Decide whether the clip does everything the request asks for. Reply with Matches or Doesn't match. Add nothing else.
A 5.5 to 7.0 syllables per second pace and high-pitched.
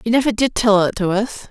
Matches